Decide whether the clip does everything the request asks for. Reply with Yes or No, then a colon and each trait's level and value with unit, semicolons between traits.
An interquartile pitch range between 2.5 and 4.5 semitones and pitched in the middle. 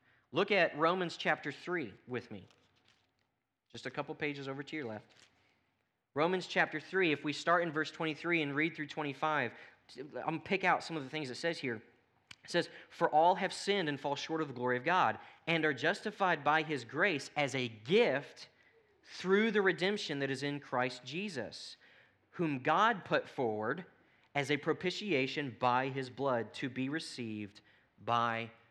No: average, 5.0 semitones; medium, 150 Hz